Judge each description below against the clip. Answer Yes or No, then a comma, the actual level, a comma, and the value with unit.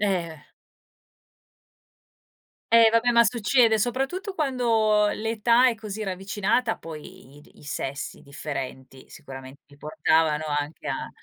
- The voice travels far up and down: Yes, wide, 7.6 semitones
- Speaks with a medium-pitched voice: No, high, 205 Hz